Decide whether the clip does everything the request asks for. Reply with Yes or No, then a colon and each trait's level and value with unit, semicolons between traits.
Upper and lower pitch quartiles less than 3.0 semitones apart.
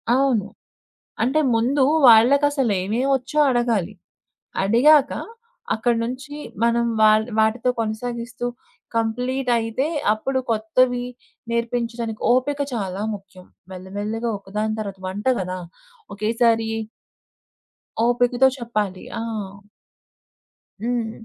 Yes: narrow, 2.6 semitones